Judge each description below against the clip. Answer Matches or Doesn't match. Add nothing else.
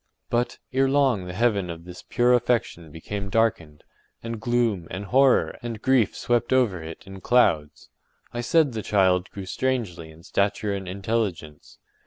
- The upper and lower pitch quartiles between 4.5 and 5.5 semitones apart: Matches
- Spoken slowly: Doesn't match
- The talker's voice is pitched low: Matches